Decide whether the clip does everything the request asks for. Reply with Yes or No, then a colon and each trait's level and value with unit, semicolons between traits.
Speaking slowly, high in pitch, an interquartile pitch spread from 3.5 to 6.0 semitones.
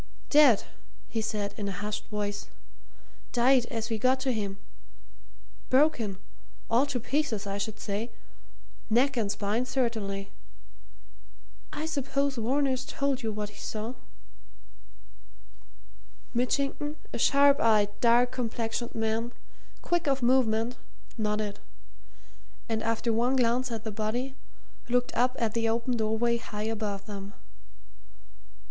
No: slow, 125 wpm; high, 230 Hz; average, 3.1 semitones